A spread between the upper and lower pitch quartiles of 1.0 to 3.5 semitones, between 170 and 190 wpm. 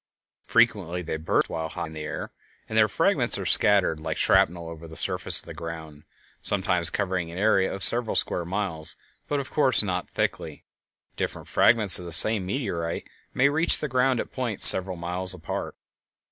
No: average, 4.7 semitones; average, 180 wpm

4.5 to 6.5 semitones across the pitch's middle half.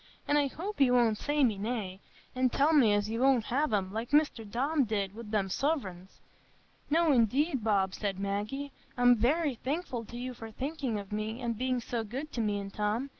Yes: average, 4.8 semitones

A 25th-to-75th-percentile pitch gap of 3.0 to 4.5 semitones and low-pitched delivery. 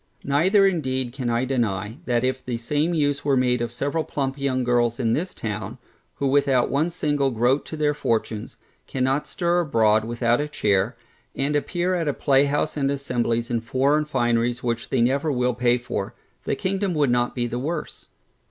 Yes: average, 3.6 semitones; low, 130 Hz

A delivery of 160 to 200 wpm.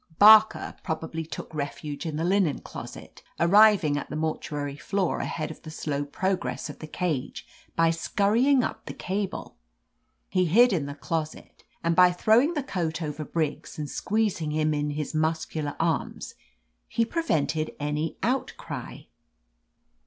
No: average, 150 wpm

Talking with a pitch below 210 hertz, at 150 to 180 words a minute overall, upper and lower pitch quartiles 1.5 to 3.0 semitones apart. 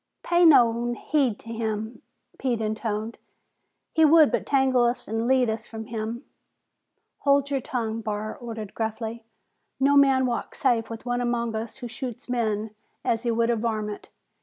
No: high, 235 Hz; average, 160 wpm; average, 2.7 semitones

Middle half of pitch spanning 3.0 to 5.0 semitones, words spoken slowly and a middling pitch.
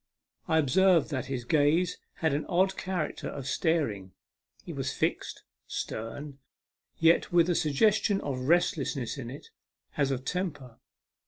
No: average, 4.7 semitones; average, 145 wpm; medium, 150 Hz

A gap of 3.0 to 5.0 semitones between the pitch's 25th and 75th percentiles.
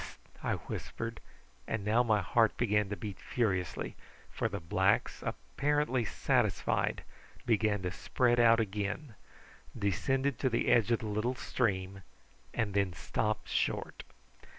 Yes: average, 3.3 semitones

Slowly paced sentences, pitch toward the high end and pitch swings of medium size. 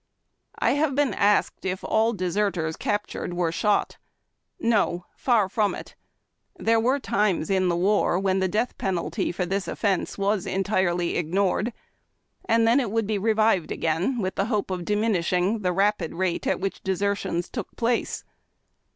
No: average, 160 wpm; high, 200 Hz; average, 3.2 semitones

